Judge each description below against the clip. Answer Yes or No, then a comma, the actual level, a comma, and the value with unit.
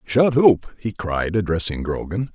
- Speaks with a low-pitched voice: Yes, low, 100 Hz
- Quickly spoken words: No, average, 155 wpm